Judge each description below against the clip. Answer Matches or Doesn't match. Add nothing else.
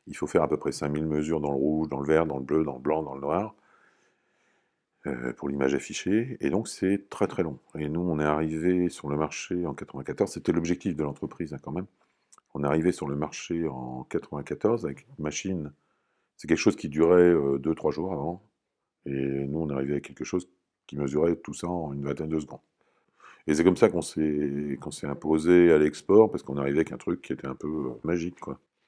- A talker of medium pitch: Doesn't match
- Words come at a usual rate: Doesn't match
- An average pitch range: Matches